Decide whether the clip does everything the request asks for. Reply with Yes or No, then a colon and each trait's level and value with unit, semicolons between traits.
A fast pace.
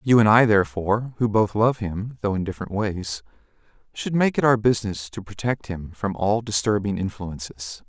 No: average, 185 wpm